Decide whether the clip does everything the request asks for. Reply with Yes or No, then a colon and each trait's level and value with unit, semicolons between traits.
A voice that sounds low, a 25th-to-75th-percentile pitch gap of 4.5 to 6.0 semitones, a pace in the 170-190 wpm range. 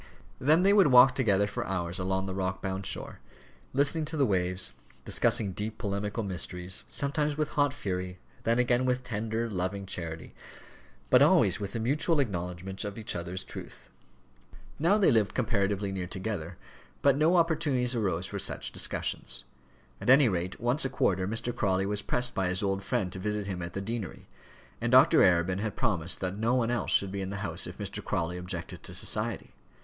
Yes: low, 100 Hz; average, 5.0 semitones; average, 185 wpm